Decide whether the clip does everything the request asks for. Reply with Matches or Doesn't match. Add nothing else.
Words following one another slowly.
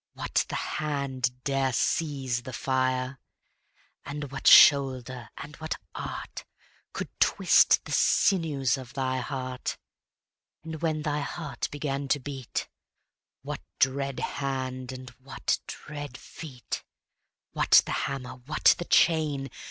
Matches